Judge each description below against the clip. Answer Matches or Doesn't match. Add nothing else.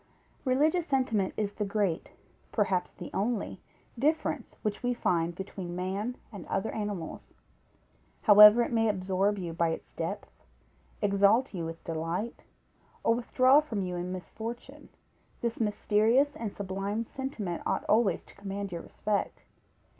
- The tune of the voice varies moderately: Matches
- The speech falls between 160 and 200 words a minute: Doesn't match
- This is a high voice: Matches